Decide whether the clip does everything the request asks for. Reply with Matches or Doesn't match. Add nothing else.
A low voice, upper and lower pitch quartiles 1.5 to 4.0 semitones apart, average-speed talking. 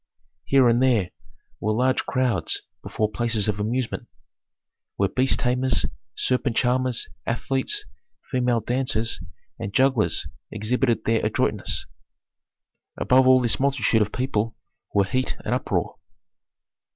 Doesn't match